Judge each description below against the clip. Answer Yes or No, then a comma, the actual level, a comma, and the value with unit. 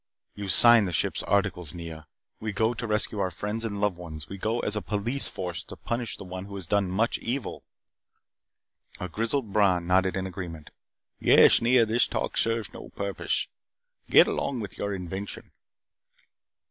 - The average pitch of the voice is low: Yes, low, 100 Hz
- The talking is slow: No, average, 170 wpm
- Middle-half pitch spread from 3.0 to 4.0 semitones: Yes, average, 3.5 semitones